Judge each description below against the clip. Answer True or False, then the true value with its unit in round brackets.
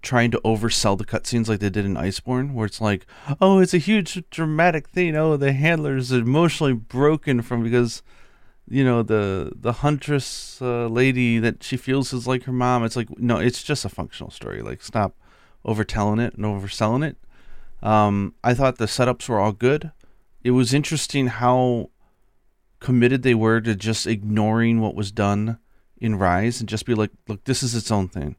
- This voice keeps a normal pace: True (190 wpm)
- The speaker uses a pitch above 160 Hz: False (120 Hz)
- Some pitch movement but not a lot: True (3.6 semitones)